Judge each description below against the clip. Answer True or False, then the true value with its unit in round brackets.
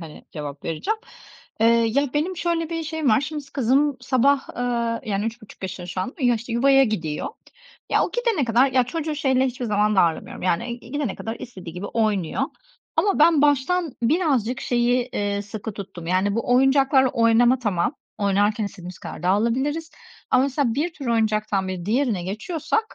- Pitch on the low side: False (240 Hz)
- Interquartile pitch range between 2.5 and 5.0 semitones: False (5.4 semitones)